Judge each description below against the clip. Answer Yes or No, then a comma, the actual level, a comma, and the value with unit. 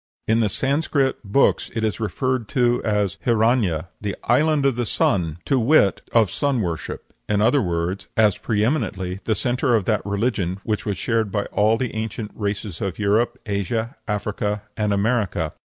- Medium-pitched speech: No, low, 110 Hz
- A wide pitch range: No, average, 3.1 semitones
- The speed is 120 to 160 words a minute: No, average, 170 wpm